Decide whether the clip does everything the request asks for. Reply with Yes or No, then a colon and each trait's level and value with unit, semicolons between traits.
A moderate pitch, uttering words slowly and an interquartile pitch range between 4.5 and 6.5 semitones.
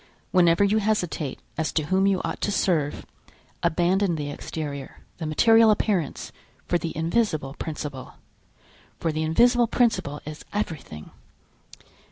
Yes: medium, 170 Hz; slow, 130 wpm; average, 5.1 semitones